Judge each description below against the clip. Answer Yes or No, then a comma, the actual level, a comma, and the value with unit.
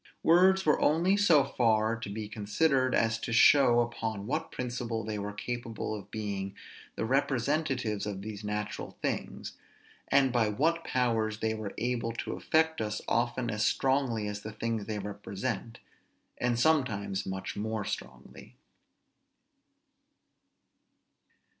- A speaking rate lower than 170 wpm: Yes, slow, 135 wpm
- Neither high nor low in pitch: No, low, 115 Hz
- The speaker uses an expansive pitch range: No, average, 3.6 semitones